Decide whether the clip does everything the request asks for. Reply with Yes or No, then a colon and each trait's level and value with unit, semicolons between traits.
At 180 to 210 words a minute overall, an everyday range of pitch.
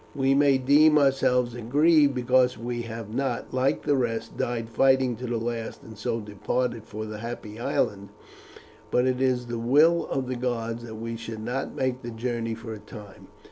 No: average, 185 wpm; narrow, 2.3 semitones